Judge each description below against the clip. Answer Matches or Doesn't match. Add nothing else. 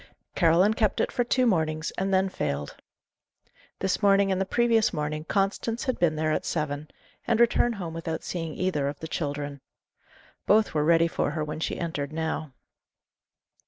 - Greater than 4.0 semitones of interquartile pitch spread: Matches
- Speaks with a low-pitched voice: Doesn't match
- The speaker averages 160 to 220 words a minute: Matches